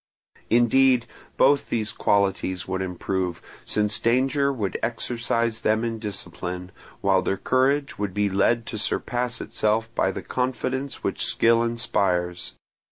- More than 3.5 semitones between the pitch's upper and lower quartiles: Yes, average, 4.3 semitones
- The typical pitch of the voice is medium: No, low, 115 Hz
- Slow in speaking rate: Yes, slow, 130 wpm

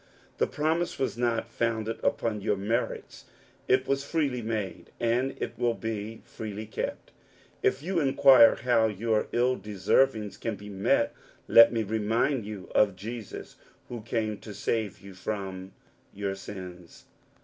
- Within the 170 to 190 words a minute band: No, average, 150 wpm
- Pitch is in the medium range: No, low, 110 Hz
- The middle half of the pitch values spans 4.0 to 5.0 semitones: No, average, 2.9 semitones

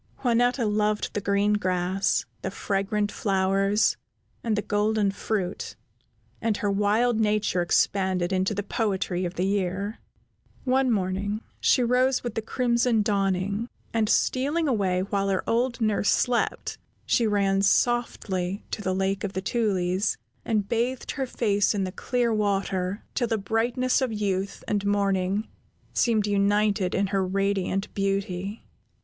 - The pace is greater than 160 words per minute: No, average, 145 wpm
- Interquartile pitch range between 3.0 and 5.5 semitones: No, narrow, 2.6 semitones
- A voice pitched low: No, high, 205 Hz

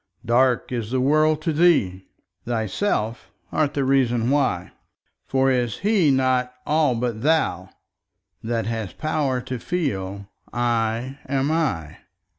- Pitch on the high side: No, low, 130 Hz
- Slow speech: Yes, slow, 120 wpm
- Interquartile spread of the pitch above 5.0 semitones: No, average, 4.3 semitones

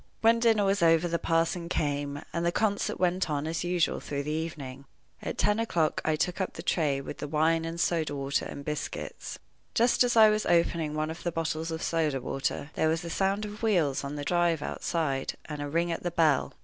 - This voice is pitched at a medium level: Yes, medium, 165 Hz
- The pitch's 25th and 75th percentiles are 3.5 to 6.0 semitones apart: No, average, 2.9 semitones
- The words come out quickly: Yes, fast, 220 wpm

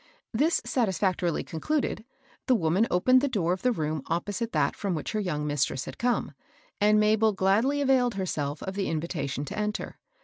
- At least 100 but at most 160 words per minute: No, average, 180 wpm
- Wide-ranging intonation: Yes, wide, 6.0 semitones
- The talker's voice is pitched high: Yes, high, 200 Hz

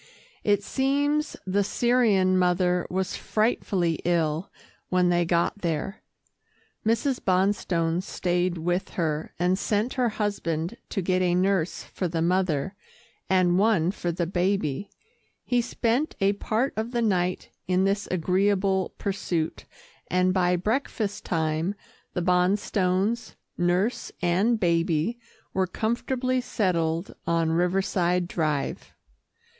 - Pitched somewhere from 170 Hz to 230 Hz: Yes, medium, 185 Hz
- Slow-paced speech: Yes, slow, 120 wpm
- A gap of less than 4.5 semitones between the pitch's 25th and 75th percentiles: Yes, average, 3.0 semitones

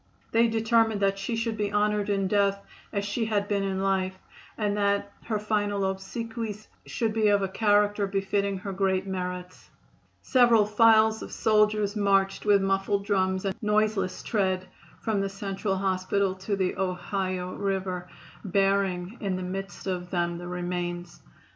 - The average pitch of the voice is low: No, high, 200 Hz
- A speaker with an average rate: Yes, average, 155 wpm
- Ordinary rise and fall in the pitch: No, narrow, 1.9 semitones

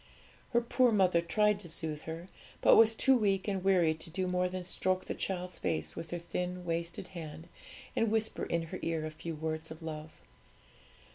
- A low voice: No, medium, 175 Hz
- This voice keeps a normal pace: Yes, average, 195 wpm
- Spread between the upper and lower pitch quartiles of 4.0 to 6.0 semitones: No, average, 3.1 semitones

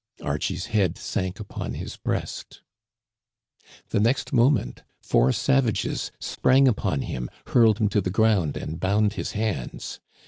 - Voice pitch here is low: Yes, low, 105 Hz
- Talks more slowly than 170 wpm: Yes, average, 140 wpm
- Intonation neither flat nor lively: Yes, average, 4.1 semitones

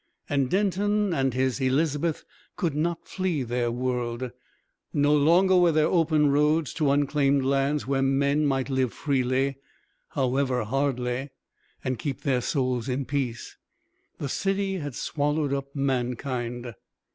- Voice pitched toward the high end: No, medium, 140 Hz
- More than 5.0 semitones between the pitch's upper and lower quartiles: No, average, 2.8 semitones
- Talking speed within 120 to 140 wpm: Yes, slow, 135 wpm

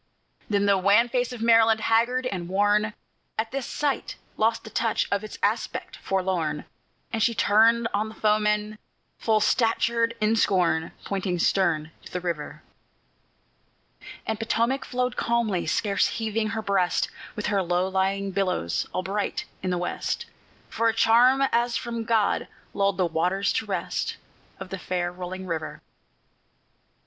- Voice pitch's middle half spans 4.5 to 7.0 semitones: No, average, 3.5 semitones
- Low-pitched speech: No, high, 210 Hz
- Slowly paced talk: No, average, 150 wpm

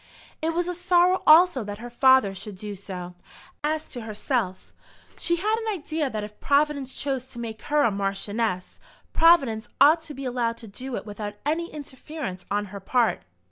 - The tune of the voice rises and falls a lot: Yes, wide, 6.8 semitones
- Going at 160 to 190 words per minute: Yes, average, 180 wpm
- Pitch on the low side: No, very high, 255 Hz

